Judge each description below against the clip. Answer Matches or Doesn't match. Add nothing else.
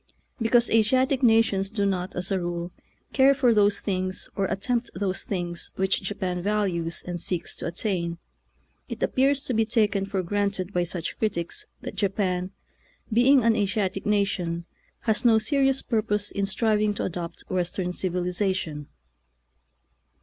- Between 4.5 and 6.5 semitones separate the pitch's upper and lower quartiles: Doesn't match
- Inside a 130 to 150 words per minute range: Matches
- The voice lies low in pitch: Doesn't match